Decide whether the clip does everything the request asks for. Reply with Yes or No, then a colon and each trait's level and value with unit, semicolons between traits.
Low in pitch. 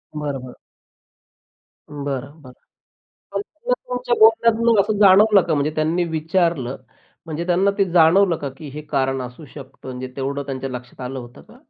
No: medium, 155 Hz